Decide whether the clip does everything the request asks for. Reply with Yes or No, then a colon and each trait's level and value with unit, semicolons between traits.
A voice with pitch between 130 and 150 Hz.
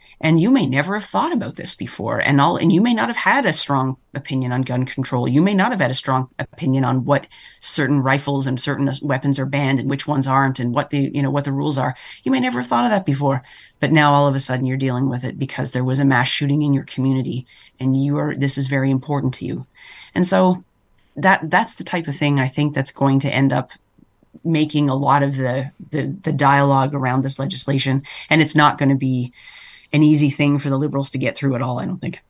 Yes: medium, 140 Hz